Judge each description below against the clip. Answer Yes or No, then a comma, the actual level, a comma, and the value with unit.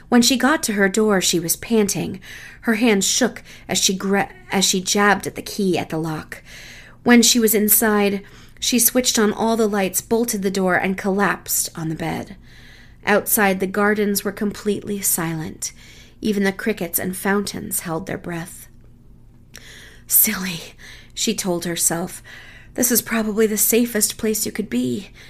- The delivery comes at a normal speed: Yes, average, 165 wpm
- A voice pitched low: No, high, 200 Hz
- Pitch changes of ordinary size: Yes, average, 3.6 semitones